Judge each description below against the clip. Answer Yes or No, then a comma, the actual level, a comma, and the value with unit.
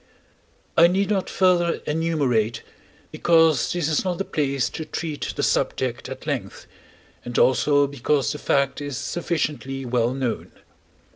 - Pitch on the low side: No, medium, 150 Hz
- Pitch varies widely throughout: No, average, 4.1 semitones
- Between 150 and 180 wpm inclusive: No, average, 140 wpm